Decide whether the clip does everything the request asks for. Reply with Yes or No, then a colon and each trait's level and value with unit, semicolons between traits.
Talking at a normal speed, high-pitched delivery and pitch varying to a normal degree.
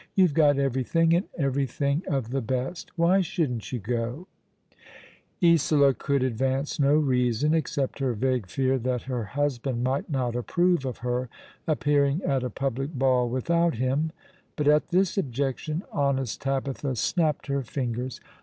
No: average, 155 wpm; low, 135 Hz; average, 3.1 semitones